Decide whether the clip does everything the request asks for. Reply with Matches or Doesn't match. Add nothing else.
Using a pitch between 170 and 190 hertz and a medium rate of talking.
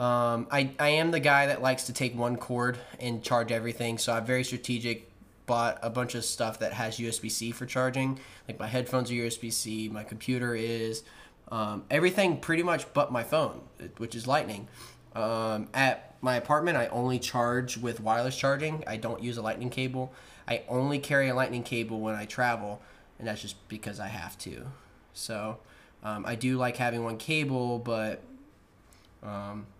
Doesn't match